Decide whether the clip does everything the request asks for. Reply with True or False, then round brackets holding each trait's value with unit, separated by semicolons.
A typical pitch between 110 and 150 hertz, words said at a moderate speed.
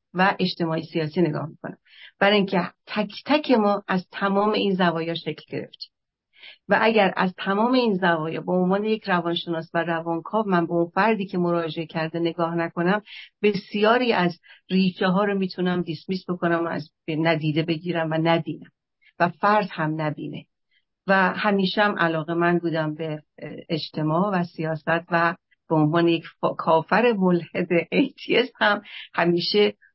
False (175 Hz; 150 wpm)